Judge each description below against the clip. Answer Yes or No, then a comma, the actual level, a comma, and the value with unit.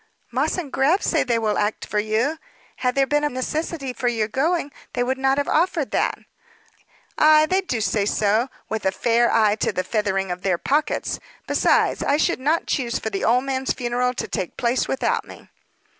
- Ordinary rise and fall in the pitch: Yes, average, 4.8 semitones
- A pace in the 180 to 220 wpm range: Yes, average, 200 wpm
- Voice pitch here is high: Yes, very high, 250 Hz